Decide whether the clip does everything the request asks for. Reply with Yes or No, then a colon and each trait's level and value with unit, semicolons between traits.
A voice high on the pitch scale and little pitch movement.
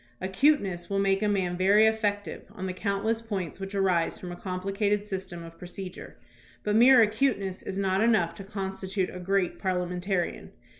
Yes: high, 195 Hz; narrow, 2.2 semitones